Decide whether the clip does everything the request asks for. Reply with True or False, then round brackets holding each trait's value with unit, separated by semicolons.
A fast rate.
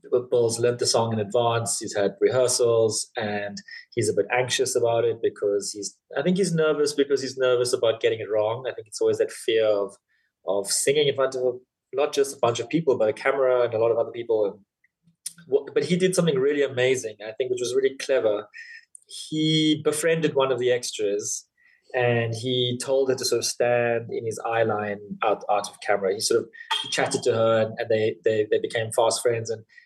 True (210 wpm)